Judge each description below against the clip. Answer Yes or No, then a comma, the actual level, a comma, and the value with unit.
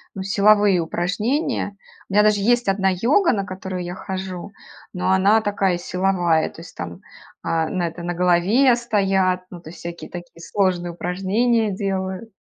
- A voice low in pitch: No, high, 190 Hz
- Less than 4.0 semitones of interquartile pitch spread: Yes, average, 2.8 semitones